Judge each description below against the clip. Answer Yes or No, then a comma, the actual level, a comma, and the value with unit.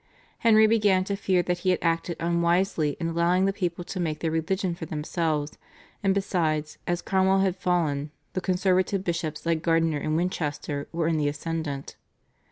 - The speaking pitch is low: No, medium, 170 Hz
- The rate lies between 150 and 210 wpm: Yes, average, 175 wpm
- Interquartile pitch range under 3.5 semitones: Yes, average, 2.8 semitones